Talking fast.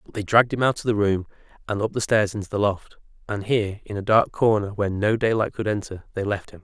Yes: fast, 260 wpm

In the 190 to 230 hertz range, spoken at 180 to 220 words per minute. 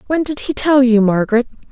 No: very high, 250 Hz; fast, 210 wpm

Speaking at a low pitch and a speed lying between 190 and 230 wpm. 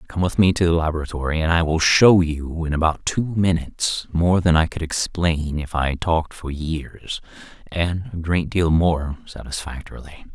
No: very low, 80 Hz; average, 180 wpm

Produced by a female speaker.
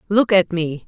Yes: female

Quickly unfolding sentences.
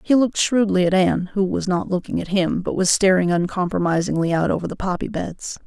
Yes: fast, 210 wpm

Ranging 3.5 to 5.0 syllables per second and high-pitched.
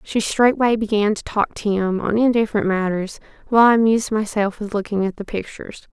No: 5.8 syllables/s; high, 210 Hz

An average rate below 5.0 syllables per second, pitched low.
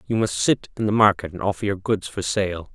No: 5.6 syllables/s; low, 100 Hz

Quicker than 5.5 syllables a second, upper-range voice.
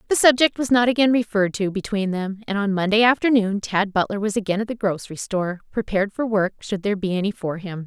Yes: 6.3 syllables/s; high, 205 Hz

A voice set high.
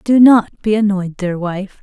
Yes: high, 200 Hz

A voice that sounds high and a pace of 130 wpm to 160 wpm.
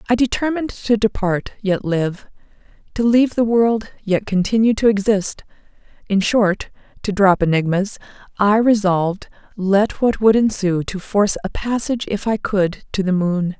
Yes: high, 205 Hz; average, 145 wpm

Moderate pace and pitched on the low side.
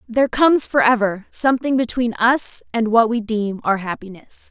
No: average, 160 wpm; high, 230 Hz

